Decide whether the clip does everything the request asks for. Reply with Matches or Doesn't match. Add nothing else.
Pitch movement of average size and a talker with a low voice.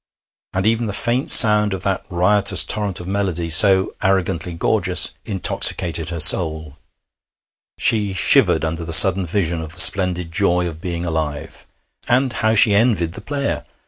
Matches